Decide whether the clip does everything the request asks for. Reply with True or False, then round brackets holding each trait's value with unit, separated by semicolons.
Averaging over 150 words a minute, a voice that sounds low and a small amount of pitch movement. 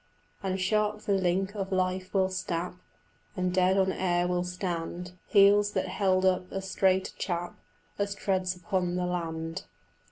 False (160 wpm; 185 Hz; 1.3 semitones)